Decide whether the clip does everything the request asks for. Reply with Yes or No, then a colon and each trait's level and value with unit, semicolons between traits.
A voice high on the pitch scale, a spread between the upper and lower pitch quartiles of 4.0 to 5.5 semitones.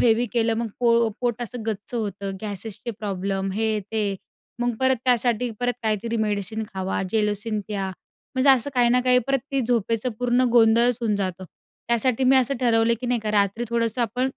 No: high, 230 Hz; average, 2.8 semitones